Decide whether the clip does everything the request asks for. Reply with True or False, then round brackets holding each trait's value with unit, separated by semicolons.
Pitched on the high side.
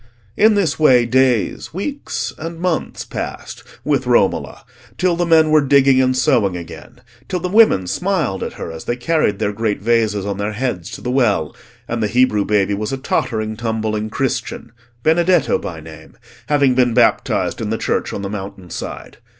False (120 Hz)